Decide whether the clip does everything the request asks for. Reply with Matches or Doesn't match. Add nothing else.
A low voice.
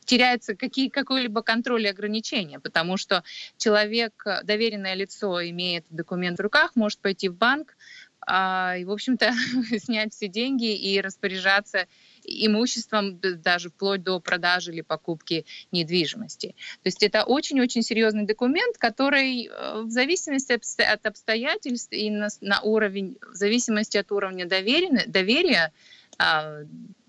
Doesn't match